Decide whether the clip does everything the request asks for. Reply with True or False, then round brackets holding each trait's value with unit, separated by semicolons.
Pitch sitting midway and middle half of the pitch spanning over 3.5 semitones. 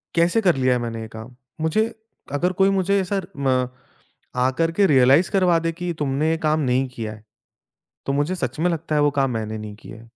True (145 Hz; 5.6 semitones)